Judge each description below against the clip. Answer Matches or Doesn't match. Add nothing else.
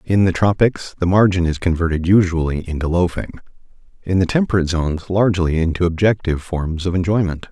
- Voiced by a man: Matches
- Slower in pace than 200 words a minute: Matches